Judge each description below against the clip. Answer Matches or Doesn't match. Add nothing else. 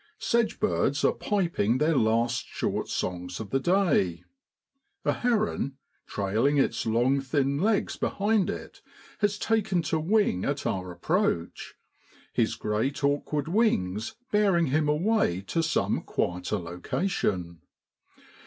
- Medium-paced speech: Doesn't match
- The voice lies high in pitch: Doesn't match